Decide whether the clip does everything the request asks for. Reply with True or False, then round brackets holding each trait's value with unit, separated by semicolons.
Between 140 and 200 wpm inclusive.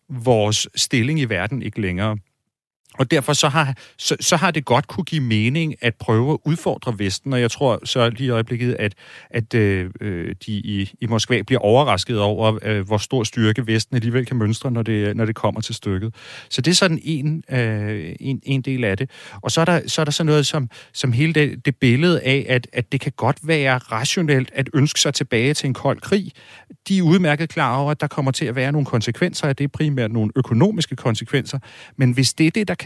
False (225 wpm)